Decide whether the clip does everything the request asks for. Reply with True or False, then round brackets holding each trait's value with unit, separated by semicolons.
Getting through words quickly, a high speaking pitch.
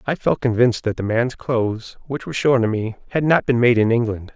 False (250 wpm; 120 Hz)